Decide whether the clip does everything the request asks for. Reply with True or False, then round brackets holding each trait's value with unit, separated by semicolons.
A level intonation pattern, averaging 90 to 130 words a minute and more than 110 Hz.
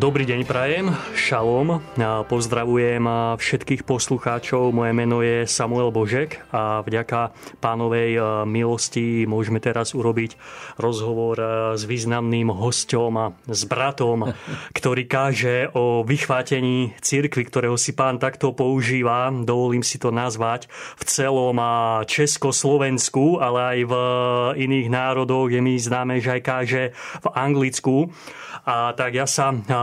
True (2.1 semitones; 120 wpm; 125 Hz)